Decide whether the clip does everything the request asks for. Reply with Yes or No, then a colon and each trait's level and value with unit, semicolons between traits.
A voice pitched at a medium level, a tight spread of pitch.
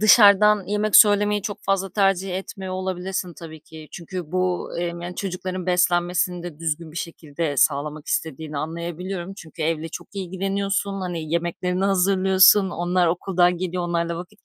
Yes: medium, 180 Hz; narrow, 2.3 semitones